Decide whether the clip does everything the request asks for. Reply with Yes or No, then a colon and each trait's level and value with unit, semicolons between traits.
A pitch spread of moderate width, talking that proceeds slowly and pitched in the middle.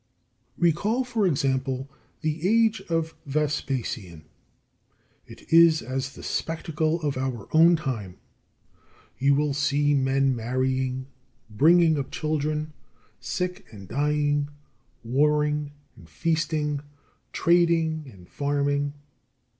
Yes: average, 3.3 semitones; slow, 105 wpm; medium, 145 Hz